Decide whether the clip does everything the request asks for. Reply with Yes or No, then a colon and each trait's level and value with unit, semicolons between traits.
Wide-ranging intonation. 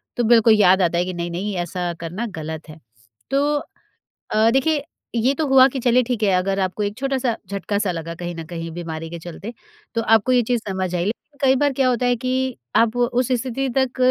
Yes: wide, 6.2 semitones